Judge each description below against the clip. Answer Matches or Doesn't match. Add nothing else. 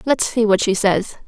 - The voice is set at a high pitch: Matches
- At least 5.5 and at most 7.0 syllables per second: Doesn't match